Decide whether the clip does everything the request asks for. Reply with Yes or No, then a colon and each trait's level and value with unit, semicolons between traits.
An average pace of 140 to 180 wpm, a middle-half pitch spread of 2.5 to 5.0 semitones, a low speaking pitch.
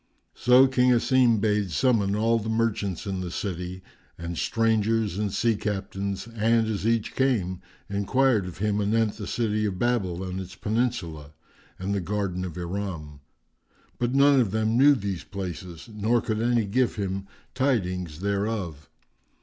Yes: average, 155 wpm; average, 3.7 semitones; low, 105 Hz